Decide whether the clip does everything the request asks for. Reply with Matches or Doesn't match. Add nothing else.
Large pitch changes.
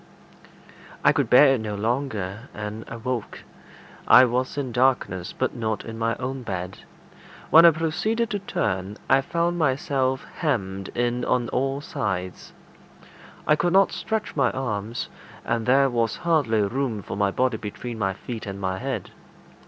Doesn't match